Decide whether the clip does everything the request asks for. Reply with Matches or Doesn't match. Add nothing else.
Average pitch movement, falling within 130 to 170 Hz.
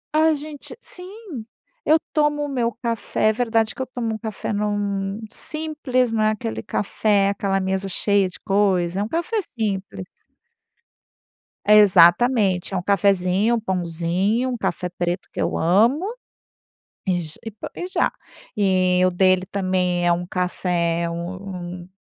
Doesn't match